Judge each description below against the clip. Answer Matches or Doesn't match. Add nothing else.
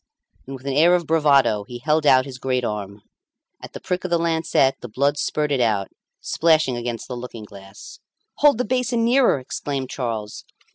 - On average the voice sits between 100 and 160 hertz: Matches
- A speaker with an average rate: Matches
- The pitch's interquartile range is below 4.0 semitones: Doesn't match